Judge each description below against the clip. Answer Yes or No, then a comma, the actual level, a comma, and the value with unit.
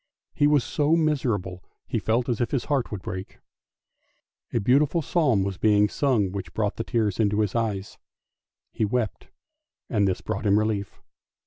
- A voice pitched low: Yes, low, 110 Hz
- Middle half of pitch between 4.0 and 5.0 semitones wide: Yes, average, 4.4 semitones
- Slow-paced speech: No, average, 170 wpm